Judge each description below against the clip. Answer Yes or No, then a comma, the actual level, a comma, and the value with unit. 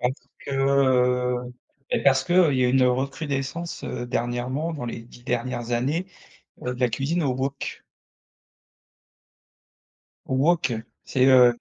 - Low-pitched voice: Yes, low, 130 Hz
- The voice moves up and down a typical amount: No, narrow, 1.9 semitones